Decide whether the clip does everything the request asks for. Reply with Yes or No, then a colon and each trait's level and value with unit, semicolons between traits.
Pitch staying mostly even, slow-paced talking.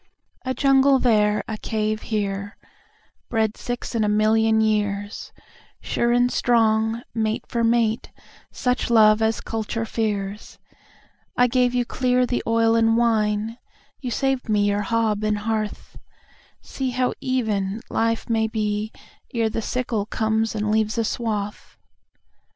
Yes: narrow, 1.9 semitones; slow, 120 wpm